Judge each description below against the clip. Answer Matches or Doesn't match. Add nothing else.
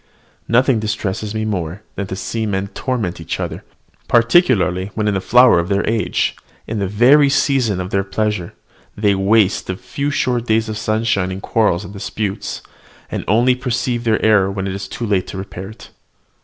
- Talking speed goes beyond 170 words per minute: Matches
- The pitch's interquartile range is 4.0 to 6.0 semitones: Doesn't match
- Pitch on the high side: Doesn't match